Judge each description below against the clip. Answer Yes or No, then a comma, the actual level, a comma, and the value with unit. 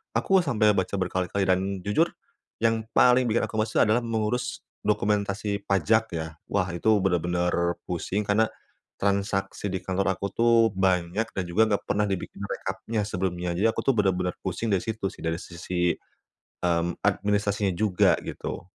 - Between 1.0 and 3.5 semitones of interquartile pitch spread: Yes, average, 3.0 semitones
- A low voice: Yes, low, 100 Hz